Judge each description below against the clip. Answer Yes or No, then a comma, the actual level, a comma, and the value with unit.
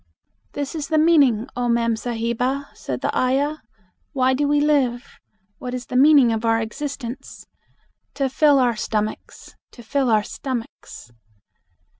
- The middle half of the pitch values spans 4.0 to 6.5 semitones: No, average, 3.5 semitones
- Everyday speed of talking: Yes, average, 145 wpm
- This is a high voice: Yes, very high, 255 Hz